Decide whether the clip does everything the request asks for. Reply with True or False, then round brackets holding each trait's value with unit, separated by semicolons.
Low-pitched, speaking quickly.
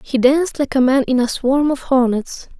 False (265 Hz; 230 wpm)